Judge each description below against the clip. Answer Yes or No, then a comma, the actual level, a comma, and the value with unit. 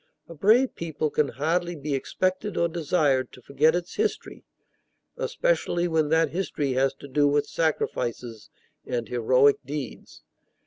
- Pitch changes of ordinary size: Yes, average, 4.1 semitones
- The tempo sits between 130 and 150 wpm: Yes, average, 140 wpm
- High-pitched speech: No, medium, 150 Hz